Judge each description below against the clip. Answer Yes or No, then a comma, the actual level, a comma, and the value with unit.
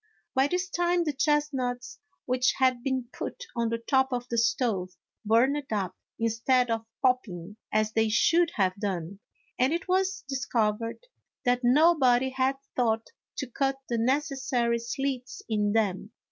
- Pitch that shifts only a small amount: No, average, 3.3 semitones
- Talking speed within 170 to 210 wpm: No, average, 150 wpm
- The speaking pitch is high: Yes, very high, 250 Hz